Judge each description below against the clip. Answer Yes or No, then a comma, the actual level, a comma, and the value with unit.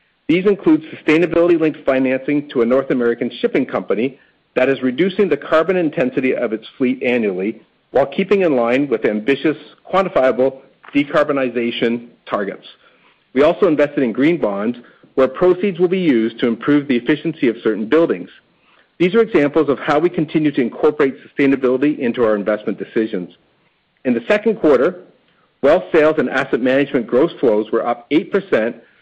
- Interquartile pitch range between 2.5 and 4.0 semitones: No, average, 5.0 semitones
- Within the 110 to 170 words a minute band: Yes, average, 155 wpm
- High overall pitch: No, medium, 140 Hz